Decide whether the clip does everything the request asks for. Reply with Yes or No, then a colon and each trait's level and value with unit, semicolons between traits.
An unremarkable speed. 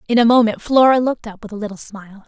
No: fast, 265 wpm